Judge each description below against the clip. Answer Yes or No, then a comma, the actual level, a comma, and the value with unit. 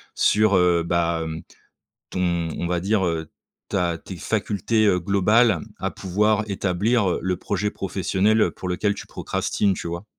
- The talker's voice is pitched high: No, very low, 95 Hz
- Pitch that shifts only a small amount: No, average, 3.2 semitones